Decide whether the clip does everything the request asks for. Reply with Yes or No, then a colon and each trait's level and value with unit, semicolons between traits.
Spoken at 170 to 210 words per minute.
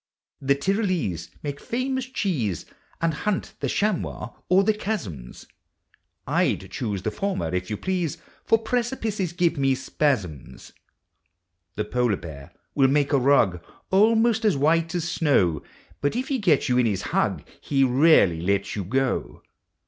No: average, 155 wpm